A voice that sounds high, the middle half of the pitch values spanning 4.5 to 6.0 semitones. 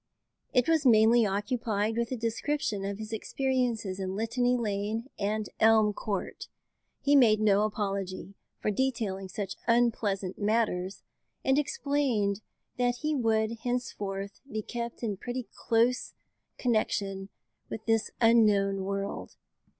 No: high, 220 Hz; average, 3.3 semitones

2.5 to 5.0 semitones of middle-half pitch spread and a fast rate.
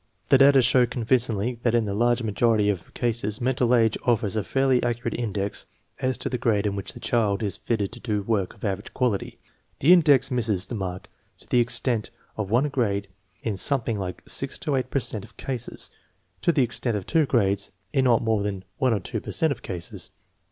Yes: average, 3.6 semitones; fast, 215 wpm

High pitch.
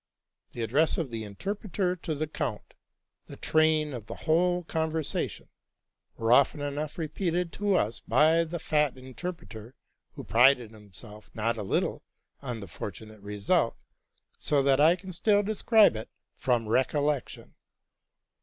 No: medium, 145 Hz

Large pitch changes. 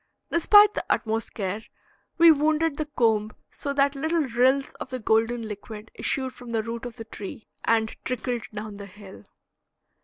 No: average, 4.2 semitones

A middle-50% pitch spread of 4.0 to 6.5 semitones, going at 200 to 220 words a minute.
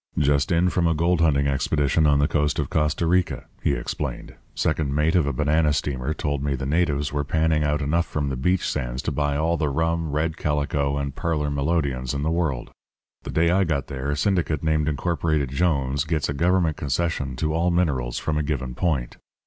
No: average, 2.7 semitones; fast, 205 wpm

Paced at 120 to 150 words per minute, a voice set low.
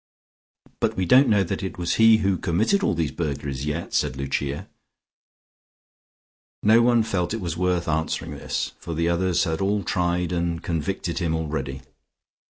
No: average, 165 wpm; very low, 85 Hz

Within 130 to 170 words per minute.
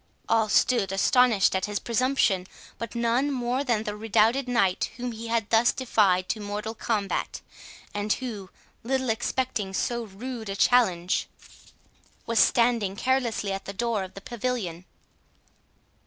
Yes: average, 140 wpm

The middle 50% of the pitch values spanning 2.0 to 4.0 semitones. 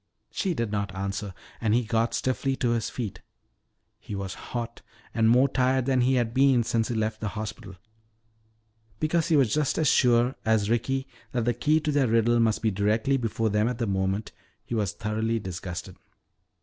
Yes: average, 3.1 semitones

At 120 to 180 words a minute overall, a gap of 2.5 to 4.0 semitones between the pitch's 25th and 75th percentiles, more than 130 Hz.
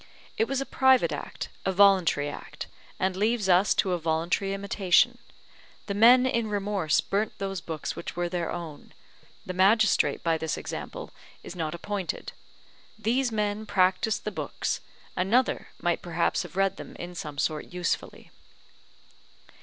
Yes: average, 150 wpm; average, 3.6 semitones; high, 190 Hz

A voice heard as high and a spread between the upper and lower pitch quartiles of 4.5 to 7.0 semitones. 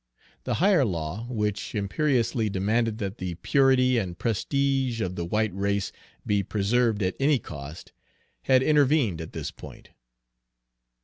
No: low, 110 Hz; average, 4.9 semitones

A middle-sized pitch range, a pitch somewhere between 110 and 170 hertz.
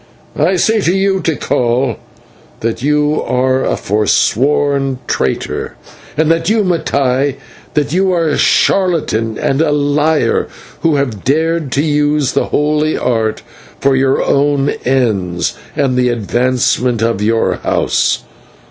Yes: average, 3.7 semitones; medium, 140 Hz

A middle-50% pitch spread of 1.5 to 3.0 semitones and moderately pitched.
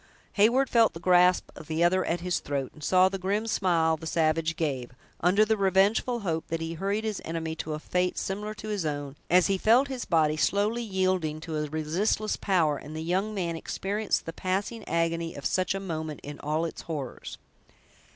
No: average, 3.9 semitones; medium, 175 Hz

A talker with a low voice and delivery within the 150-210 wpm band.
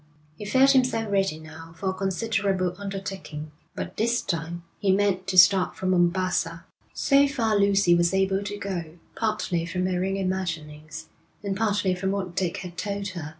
No: high, 190 Hz; average, 170 wpm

